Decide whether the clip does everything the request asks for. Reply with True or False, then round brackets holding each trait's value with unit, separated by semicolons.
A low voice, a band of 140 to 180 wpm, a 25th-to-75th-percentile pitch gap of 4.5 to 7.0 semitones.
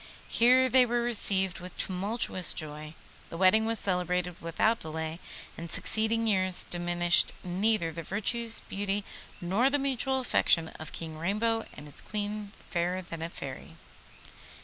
False (190 Hz; 145 wpm; 4.8 semitones)